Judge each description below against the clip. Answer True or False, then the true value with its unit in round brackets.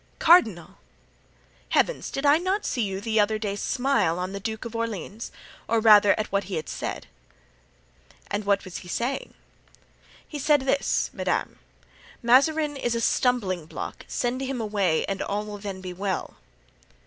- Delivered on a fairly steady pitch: False (4.6 semitones)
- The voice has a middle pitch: False (220 Hz)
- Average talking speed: True (160 wpm)